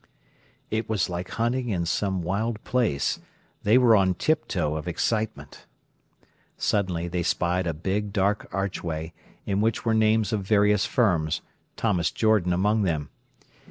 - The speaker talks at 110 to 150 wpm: Yes, average, 140 wpm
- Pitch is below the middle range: Yes, low, 100 Hz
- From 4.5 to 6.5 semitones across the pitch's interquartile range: No, average, 4.0 semitones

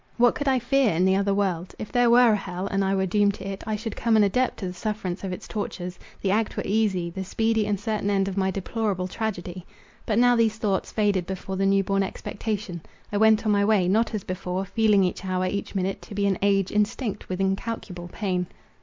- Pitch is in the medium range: No, high, 200 Hz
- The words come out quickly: Yes, fast, 235 wpm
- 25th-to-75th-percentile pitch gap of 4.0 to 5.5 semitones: No, narrow, 2.5 semitones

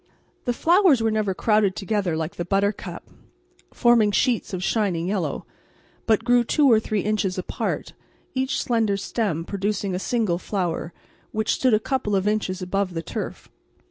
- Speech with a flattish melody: No, average, 3.4 semitones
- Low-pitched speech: No, high, 205 Hz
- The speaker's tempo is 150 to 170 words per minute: Yes, average, 160 wpm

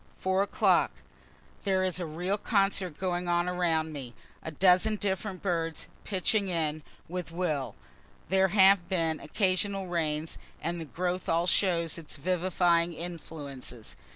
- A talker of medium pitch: Yes, medium, 175 Hz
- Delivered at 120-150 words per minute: Yes, average, 140 wpm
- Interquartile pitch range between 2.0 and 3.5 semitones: Yes, narrow, 2.5 semitones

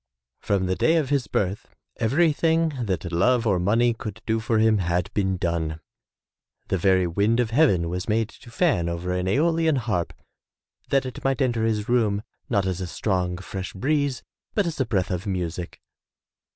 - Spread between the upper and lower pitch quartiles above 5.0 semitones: Yes, wide, 5.6 semitones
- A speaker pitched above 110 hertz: No, low, 105 Hz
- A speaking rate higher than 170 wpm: Yes, average, 180 wpm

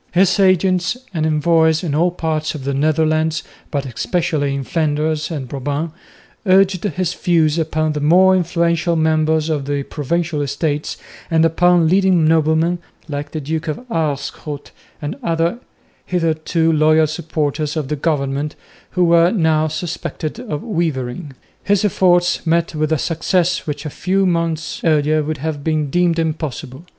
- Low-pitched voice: No, medium, 160 Hz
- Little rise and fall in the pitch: Yes, narrow, 2.2 semitones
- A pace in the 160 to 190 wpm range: No, average, 150 wpm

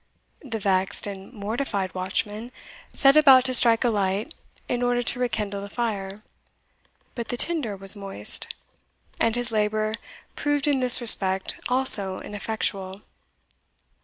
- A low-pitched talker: No, high, 215 Hz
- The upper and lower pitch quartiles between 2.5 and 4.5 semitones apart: Yes, average, 3.8 semitones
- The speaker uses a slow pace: Yes, slow, 130 wpm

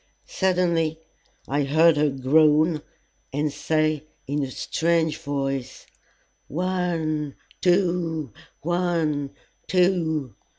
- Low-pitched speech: No, medium, 155 Hz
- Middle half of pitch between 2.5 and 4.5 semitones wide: Yes, average, 2.8 semitones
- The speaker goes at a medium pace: No, slow, 85 wpm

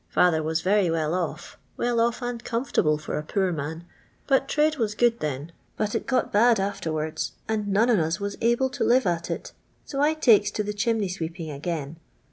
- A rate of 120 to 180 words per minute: No, average, 200 wpm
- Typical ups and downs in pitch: No, wide, 6.4 semitones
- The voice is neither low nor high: No, high, 200 Hz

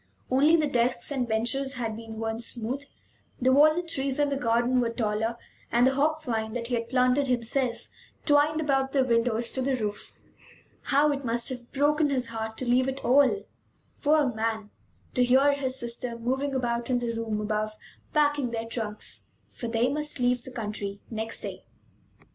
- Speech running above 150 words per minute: Yes, average, 180 wpm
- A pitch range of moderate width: Yes, average, 3.2 semitones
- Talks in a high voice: Yes, very high, 250 Hz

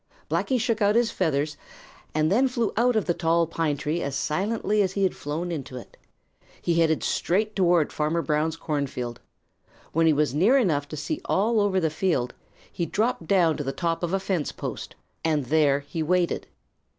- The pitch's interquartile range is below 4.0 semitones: No, average, 4.6 semitones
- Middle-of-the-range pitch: Yes, medium, 165 Hz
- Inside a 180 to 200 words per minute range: Yes, average, 190 wpm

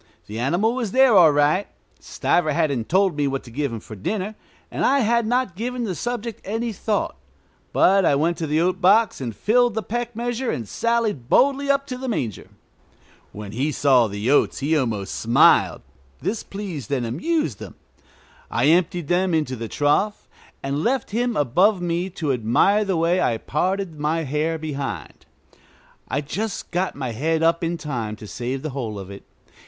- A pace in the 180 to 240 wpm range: Yes, average, 185 wpm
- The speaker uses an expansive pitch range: Yes, wide, 7.7 semitones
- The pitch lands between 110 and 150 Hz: No, medium, 165 Hz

